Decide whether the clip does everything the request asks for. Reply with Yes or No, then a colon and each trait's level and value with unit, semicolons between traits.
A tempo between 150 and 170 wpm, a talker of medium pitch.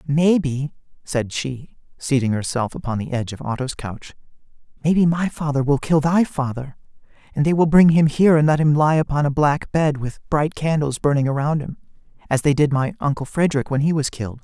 No: average, 200 wpm; medium, 145 Hz